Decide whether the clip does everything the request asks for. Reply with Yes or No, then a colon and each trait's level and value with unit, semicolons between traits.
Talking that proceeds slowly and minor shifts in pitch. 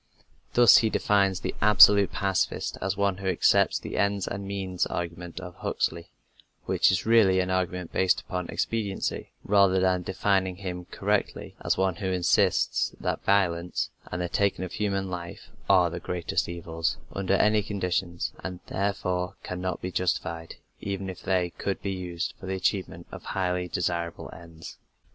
No: average, 160 wpm; narrow, 1.8 semitones